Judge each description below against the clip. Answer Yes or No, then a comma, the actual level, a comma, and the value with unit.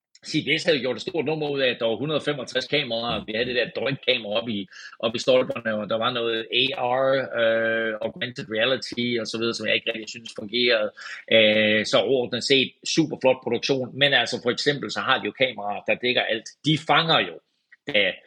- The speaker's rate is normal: Yes, average, 210 wpm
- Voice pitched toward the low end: Yes, low, 120 Hz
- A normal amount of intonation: Yes, average, 3.7 semitones